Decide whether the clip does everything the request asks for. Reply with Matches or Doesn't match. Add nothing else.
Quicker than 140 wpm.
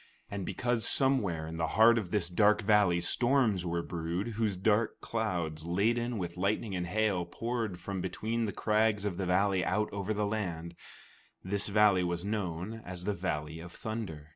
Matches